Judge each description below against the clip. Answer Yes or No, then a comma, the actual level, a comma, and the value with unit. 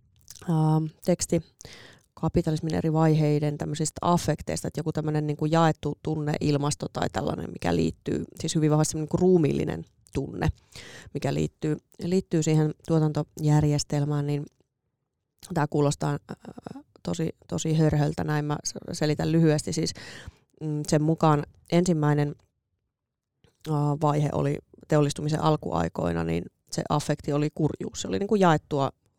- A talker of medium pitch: Yes, medium, 150 Hz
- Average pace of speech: Yes, average, 115 wpm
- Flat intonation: Yes, narrow, 1.6 semitones